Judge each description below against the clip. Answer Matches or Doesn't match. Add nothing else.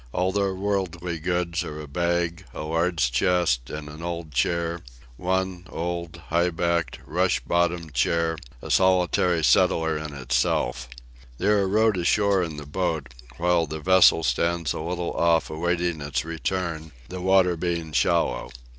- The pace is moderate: Matches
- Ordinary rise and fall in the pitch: Doesn't match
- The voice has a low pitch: Matches